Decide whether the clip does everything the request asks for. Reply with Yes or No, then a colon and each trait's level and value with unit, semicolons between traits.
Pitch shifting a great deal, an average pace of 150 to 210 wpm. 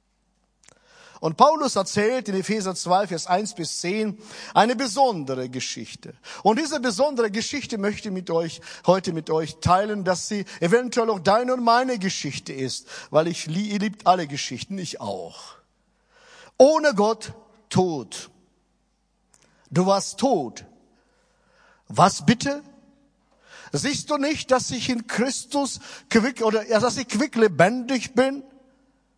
No: wide, 6.1 semitones; average, 135 wpm